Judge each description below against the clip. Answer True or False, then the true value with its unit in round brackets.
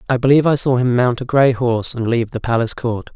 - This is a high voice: False (125 Hz)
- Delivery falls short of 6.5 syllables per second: False (6.8 syllables/s)